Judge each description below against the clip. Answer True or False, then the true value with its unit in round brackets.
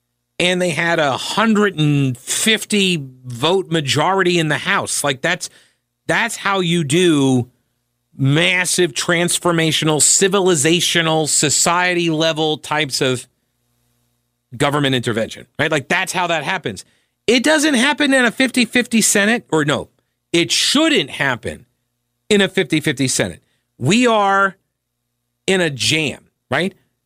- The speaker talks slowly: True (120 wpm)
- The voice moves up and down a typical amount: False (6.6 semitones)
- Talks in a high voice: False (160 Hz)